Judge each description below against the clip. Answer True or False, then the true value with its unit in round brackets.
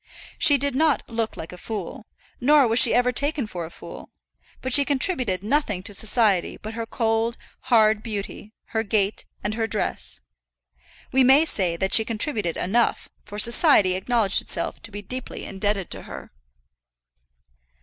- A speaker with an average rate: True (160 wpm)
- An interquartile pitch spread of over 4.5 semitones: False (3.8 semitones)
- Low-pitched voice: False (225 Hz)